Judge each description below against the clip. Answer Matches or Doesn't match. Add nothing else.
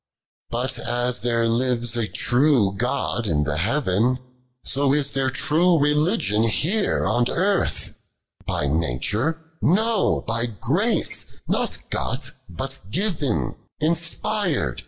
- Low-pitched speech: Matches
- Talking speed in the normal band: Doesn't match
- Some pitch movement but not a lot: Doesn't match